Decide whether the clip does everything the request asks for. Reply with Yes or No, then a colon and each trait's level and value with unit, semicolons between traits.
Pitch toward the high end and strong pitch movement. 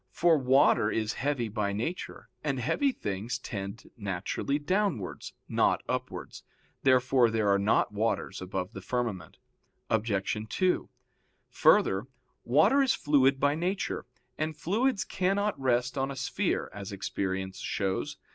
No: low, 125 Hz; wide, 6.7 semitones